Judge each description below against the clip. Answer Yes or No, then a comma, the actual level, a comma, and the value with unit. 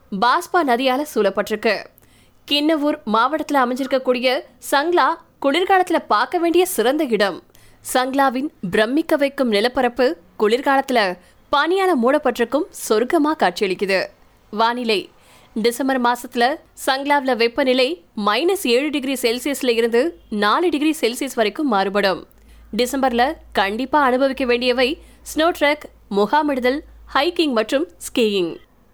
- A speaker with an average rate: Yes, average, 95 wpm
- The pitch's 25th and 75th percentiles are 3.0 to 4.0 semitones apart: No, average, 4.4 semitones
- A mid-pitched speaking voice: No, very high, 260 Hz